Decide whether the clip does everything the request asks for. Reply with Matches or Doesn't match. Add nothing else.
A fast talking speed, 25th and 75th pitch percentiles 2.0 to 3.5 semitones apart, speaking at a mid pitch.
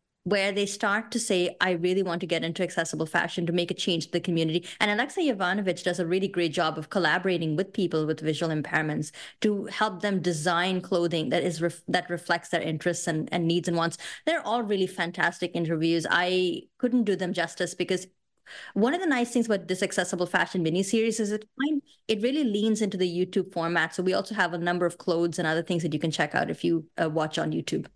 Matches